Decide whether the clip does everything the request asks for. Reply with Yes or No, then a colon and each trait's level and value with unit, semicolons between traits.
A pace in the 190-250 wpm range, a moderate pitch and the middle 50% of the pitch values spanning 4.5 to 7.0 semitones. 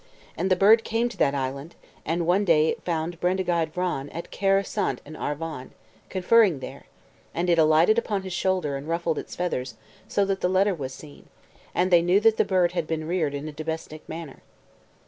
No: average, 200 wpm; medium, 170 Hz; average, 3.3 semitones